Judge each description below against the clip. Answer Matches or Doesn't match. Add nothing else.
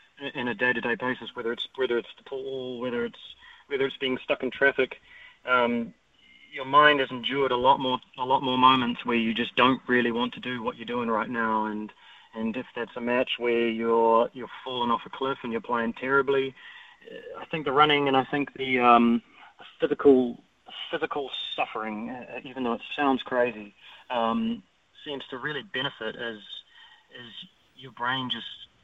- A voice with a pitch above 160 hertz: Doesn't match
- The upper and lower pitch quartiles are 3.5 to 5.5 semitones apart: Doesn't match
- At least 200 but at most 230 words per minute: Doesn't match